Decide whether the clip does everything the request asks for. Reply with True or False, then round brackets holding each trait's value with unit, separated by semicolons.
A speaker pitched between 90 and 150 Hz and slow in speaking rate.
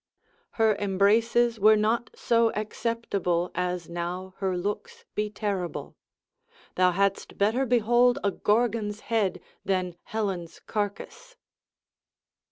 False (210 Hz; 105 wpm)